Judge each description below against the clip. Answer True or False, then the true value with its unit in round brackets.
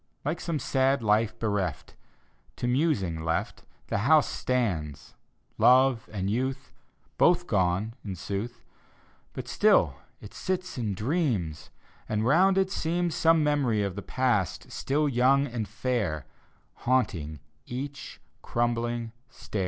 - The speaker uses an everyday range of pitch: False (5.7 semitones)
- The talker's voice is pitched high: False (120 Hz)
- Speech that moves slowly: True (125 wpm)